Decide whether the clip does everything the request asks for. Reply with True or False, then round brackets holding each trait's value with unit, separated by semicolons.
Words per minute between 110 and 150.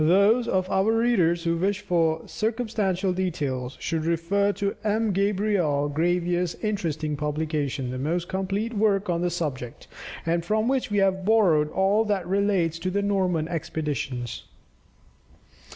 True (140 wpm)